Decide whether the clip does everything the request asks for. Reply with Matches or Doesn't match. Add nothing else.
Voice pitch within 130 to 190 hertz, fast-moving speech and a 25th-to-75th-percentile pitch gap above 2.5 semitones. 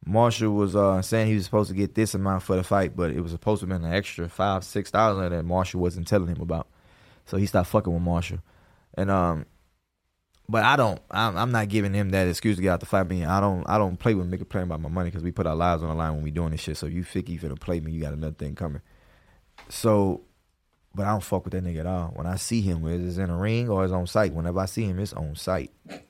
Doesn't match